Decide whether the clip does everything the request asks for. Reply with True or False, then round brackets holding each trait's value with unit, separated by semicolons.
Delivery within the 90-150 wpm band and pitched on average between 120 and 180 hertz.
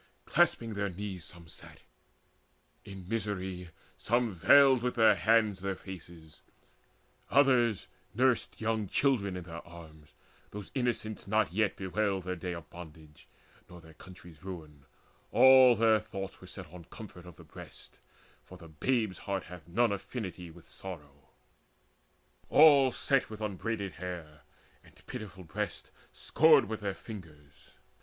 False (140 wpm; 95 Hz)